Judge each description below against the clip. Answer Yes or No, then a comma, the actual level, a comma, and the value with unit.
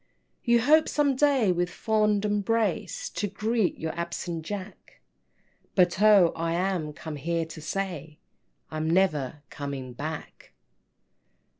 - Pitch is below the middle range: No, medium, 180 Hz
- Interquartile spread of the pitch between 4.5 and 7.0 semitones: Yes, average, 5.0 semitones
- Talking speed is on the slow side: Yes, slow, 130 wpm